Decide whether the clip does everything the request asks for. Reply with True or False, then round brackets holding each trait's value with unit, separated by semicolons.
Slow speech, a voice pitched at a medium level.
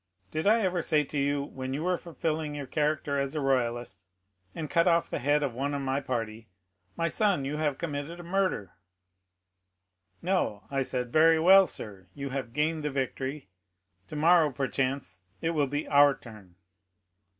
False (175 wpm; 145 Hz)